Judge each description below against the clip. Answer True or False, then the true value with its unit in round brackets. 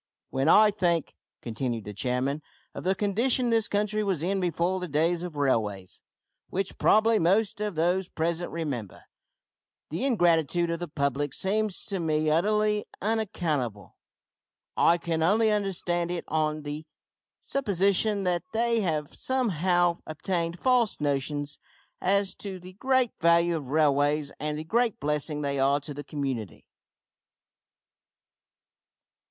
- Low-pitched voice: False (170 Hz)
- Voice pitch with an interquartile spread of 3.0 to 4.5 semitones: False (5.2 semitones)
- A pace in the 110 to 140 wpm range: True (135 wpm)